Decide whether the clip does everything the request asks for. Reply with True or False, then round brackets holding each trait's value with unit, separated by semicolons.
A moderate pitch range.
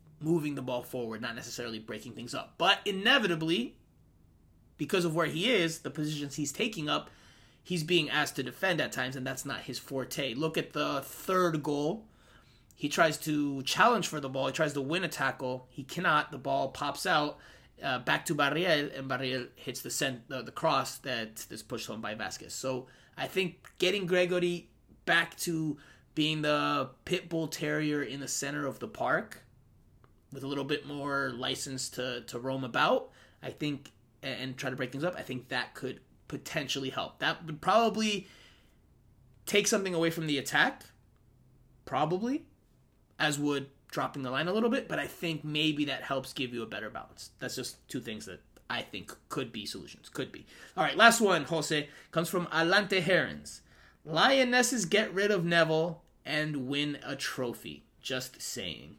True (4.3 semitones)